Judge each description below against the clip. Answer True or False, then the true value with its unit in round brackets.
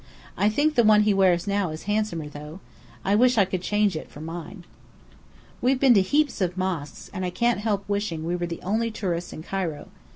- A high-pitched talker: True (195 Hz)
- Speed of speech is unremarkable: False (220 wpm)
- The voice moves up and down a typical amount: True (3.6 semitones)